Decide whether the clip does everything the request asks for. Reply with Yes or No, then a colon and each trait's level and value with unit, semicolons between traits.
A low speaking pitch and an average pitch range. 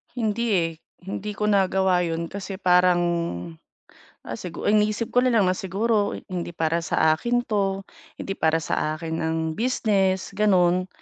No: high, 190 Hz; average, 3.4 semitones